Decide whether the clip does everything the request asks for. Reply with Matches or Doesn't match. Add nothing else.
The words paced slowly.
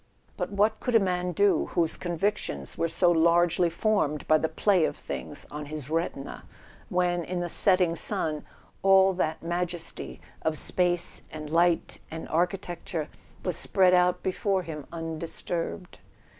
Doesn't match